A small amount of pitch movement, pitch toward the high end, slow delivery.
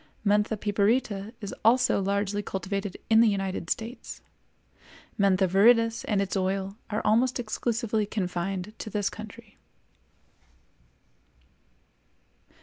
Yes: narrow, 2.2 semitones; high, 205 Hz; slow, 105 wpm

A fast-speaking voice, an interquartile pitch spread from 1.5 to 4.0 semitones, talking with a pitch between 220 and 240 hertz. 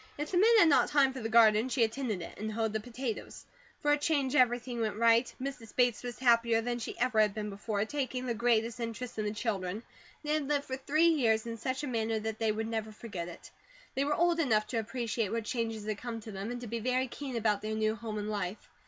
Yes: fast, 250 wpm; average, 3.1 semitones; high, 230 Hz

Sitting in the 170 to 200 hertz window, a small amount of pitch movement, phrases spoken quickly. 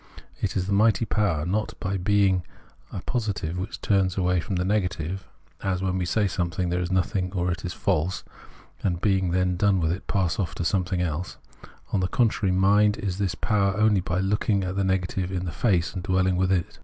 No: very low, 95 Hz; narrow, 1.7 semitones; fast, 210 wpm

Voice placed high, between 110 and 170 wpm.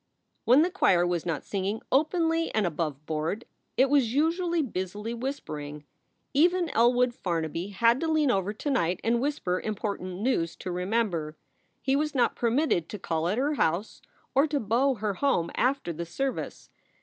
Yes: high, 225 Hz; average, 160 wpm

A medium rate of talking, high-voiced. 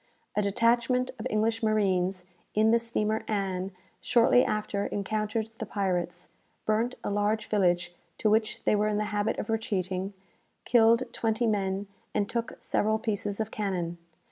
Yes: average, 150 wpm; high, 215 Hz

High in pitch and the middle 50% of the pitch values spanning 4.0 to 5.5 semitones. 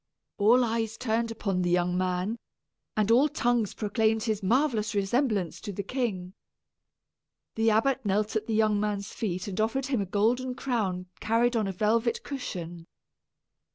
No: high, 220 Hz; average, 3.1 semitones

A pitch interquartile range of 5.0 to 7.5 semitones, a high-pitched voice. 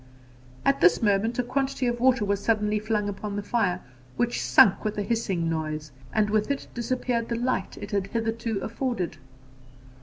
No: average, 3.3 semitones; high, 215 Hz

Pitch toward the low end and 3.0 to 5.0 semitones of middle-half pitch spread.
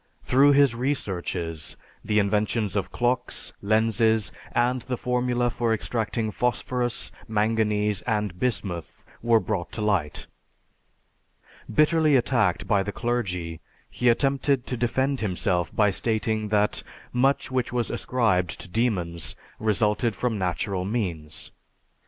Yes: low, 110 Hz; average, 3.6 semitones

